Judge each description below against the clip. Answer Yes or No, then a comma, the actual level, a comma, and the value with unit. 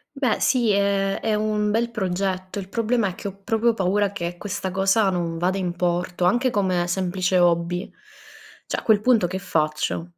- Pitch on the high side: Yes, high, 195 Hz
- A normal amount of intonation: Yes, average, 3.0 semitones